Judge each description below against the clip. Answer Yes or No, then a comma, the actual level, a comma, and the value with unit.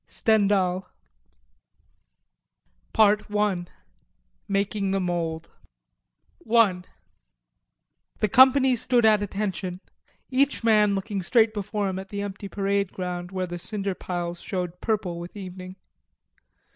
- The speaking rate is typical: No, slow, 110 wpm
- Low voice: No, high, 195 Hz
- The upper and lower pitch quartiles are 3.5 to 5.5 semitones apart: No, narrow, 2.6 semitones